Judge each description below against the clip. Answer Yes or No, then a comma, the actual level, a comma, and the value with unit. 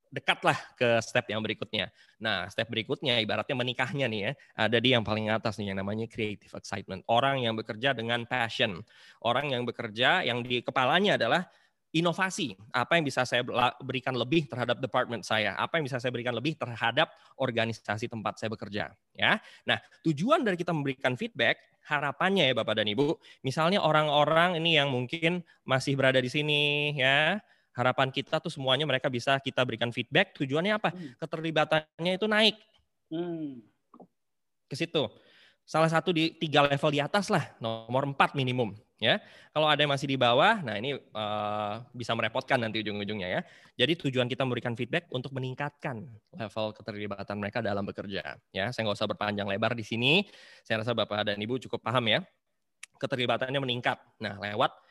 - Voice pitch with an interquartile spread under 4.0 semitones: No, average, 5.0 semitones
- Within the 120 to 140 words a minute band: No, average, 165 wpm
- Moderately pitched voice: No, low, 130 Hz